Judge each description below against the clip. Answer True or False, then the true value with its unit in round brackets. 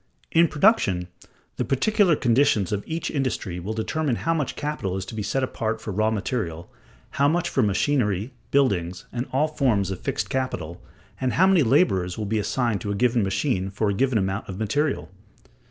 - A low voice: True (115 Hz)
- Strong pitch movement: True (6.3 semitones)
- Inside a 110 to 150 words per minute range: False (185 wpm)